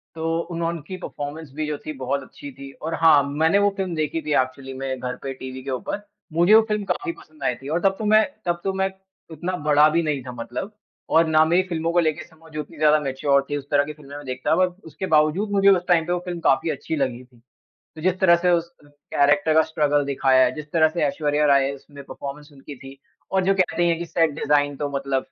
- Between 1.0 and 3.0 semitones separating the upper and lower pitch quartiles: No, average, 3.5 semitones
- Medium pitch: Yes, medium, 155 Hz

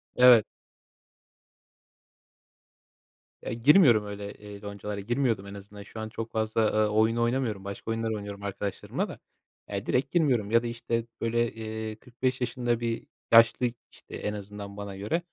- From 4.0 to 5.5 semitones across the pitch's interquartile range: No, narrow, 2.5 semitones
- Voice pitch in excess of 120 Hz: No, low, 110 Hz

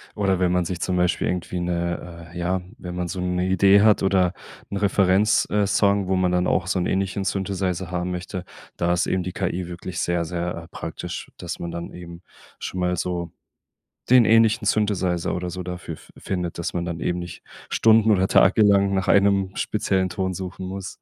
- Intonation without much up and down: Yes, narrow, 1.8 semitones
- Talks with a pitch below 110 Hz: Yes, very low, 90 Hz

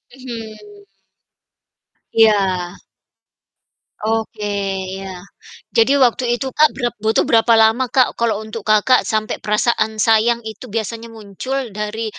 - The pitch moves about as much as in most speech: No, narrow, 1.9 semitones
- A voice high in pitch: Yes, high, 220 Hz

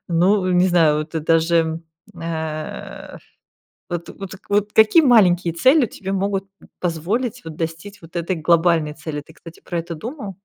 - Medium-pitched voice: Yes, medium, 175 Hz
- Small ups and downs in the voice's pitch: No, average, 3.5 semitones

